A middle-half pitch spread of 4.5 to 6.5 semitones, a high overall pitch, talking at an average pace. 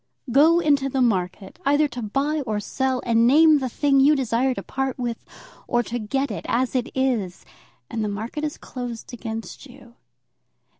No: average, 3.2 semitones; very high, 255 Hz; average, 170 wpm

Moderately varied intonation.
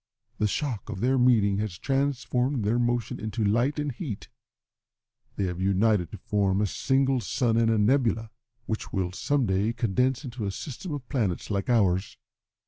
Yes: average, 4.3 semitones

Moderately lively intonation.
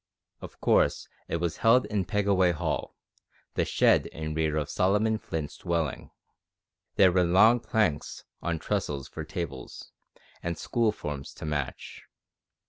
Yes: average, 4.9 semitones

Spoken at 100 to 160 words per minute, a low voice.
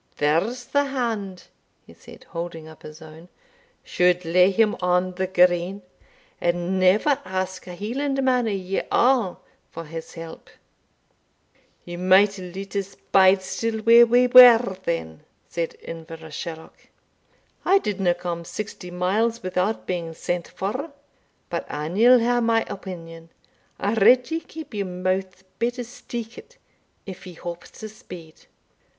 No: average, 140 wpm; high, 190 Hz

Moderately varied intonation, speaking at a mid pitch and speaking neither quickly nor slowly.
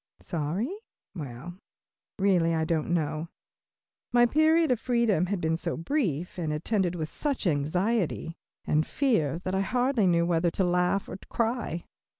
No: wide, 5.9 semitones; medium, 180 Hz; average, 150 wpm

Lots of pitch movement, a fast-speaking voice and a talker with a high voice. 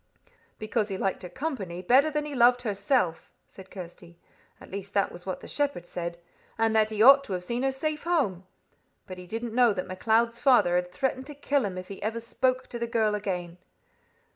Yes: wide, 5.8 semitones; fast, 210 wpm; high, 220 Hz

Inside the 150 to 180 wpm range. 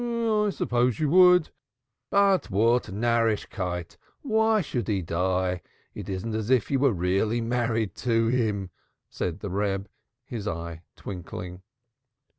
No: slow, 135 wpm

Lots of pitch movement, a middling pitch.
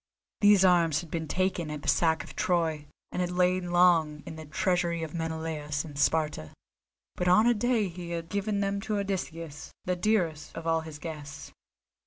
No: narrow, 2.6 semitones; medium, 170 Hz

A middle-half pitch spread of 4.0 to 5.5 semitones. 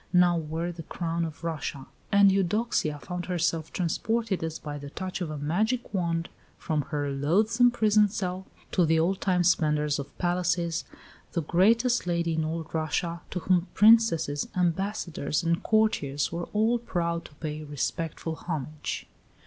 No: average, 3.4 semitones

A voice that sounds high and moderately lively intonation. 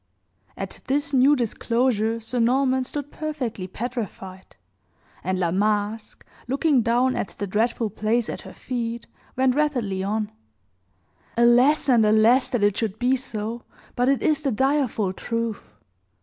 Yes: high, 235 Hz; average, 3.4 semitones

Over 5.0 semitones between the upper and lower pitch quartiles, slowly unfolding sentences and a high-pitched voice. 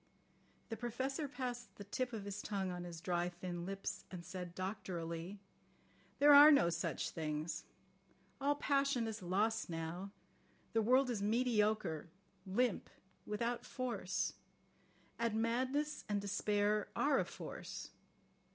Yes: wide, 5.5 semitones; slow, 130 wpm; high, 210 Hz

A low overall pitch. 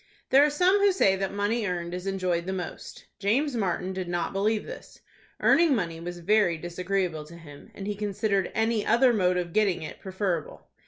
No: high, 195 Hz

